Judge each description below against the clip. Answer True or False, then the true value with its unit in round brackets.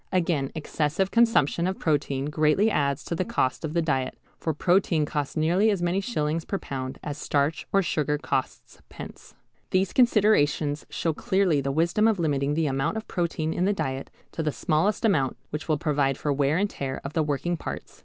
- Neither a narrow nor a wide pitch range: True (4.2 semitones)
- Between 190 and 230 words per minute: True (195 wpm)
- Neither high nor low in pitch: True (155 Hz)